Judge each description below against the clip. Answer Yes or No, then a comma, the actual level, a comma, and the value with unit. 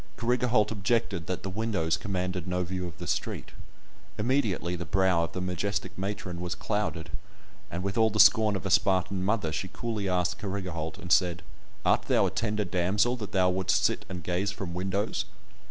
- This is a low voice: Yes, very low, 95 Hz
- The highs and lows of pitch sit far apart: No, average, 2.7 semitones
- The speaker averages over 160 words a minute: Yes, average, 185 wpm